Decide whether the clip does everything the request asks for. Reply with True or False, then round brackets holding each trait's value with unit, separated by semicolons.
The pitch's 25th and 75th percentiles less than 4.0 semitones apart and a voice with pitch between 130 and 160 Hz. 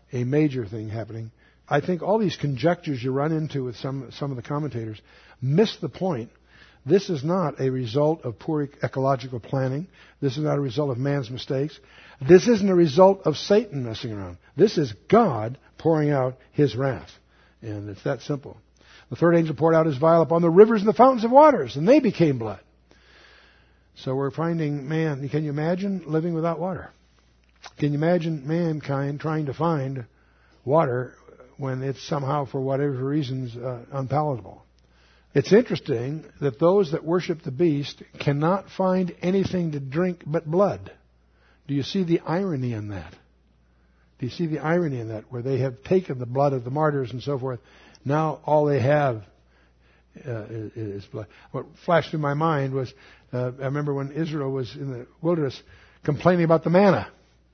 False (5.1 semitones; 140 Hz)